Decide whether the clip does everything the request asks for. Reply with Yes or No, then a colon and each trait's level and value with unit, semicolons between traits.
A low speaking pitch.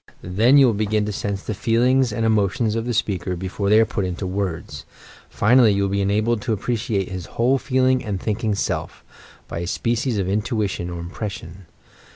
Yes: low, 105 Hz